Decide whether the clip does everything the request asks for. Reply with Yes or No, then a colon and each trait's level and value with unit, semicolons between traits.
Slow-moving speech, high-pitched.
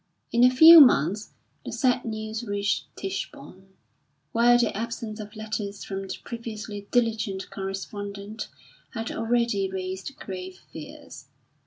Yes: slow, 125 wpm; high, 215 Hz